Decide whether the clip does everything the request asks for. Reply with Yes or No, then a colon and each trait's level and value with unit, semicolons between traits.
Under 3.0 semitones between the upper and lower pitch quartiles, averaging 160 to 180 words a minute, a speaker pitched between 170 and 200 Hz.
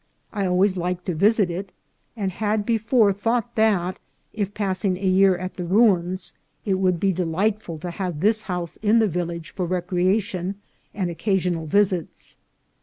Yes: narrow, 2.6 semitones; average, 165 wpm; high, 190 Hz